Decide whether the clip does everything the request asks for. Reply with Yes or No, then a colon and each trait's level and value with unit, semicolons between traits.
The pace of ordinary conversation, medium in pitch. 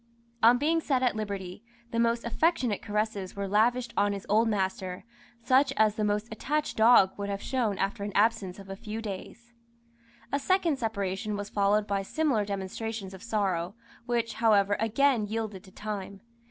No: average, 170 wpm; high, 215 Hz